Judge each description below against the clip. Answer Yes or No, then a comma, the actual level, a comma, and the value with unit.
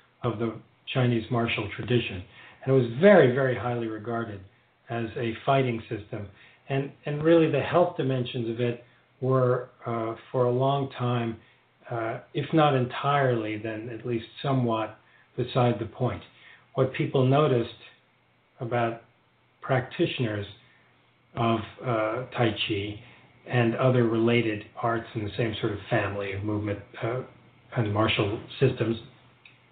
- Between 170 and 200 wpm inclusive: No, slow, 135 wpm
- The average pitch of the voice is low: Yes, low, 120 Hz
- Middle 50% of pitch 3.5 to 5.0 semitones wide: No, narrow, 2.4 semitones